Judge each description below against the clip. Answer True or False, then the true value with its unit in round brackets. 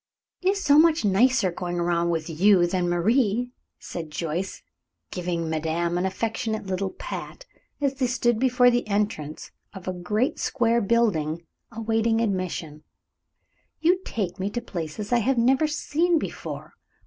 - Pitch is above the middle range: True (205 Hz)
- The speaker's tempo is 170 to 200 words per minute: False (150 wpm)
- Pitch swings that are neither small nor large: False (6.0 semitones)